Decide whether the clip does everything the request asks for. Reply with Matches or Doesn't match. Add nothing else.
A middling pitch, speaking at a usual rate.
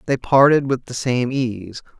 Doesn't match